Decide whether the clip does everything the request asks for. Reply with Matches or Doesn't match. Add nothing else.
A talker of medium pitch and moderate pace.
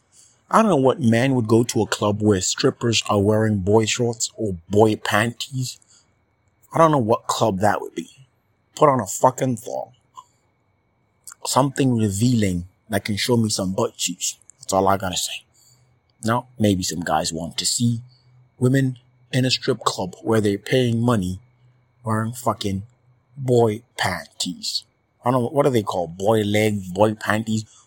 Doesn't match